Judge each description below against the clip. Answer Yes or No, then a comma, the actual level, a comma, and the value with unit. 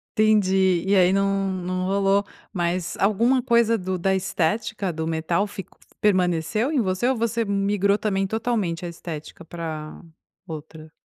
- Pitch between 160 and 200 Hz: Yes, high, 190 Hz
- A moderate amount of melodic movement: Yes, average, 3.4 semitones